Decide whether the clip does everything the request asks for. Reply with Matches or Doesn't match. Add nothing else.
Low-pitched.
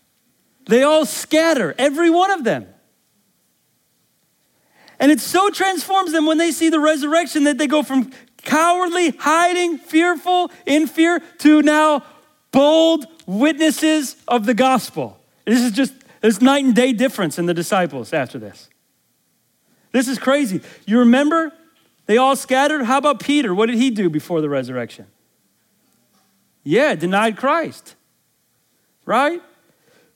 Doesn't match